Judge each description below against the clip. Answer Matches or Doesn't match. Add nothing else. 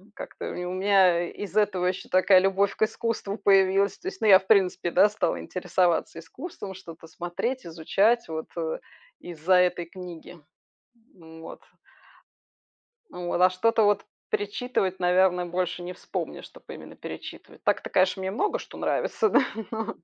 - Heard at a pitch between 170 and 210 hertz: Matches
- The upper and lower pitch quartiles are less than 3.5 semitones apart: Matches